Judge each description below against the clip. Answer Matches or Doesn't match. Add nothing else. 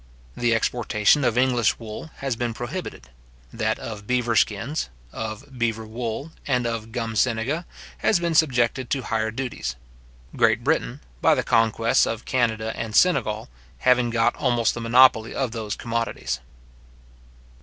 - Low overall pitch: Matches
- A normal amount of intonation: Doesn't match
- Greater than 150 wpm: Doesn't match